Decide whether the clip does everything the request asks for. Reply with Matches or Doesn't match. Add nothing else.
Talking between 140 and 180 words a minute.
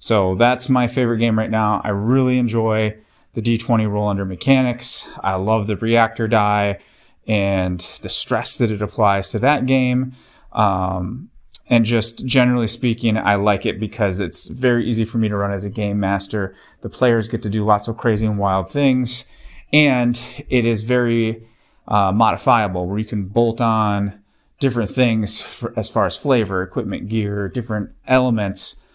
Matches